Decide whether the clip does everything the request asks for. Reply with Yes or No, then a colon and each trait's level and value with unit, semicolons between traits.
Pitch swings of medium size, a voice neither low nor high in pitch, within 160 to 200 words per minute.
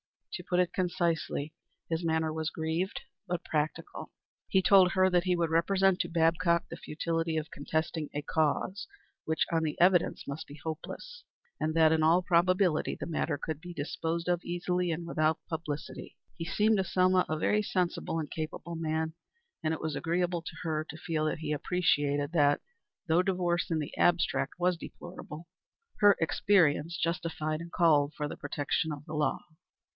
No: narrow, 2.2 semitones; medium, 165 Hz; average, 175 wpm